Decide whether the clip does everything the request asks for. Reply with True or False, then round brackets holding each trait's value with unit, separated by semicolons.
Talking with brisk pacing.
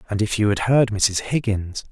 True (220 wpm)